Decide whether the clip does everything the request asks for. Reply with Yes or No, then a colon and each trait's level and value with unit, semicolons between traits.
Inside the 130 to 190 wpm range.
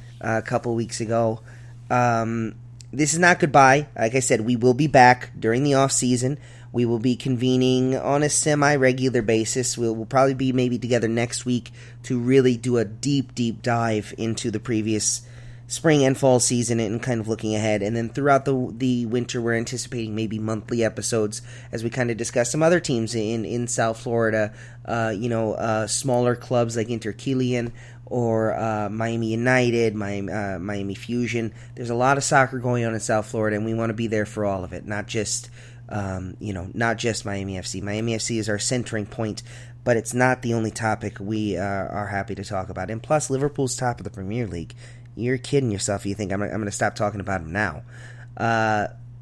No: fast, 205 wpm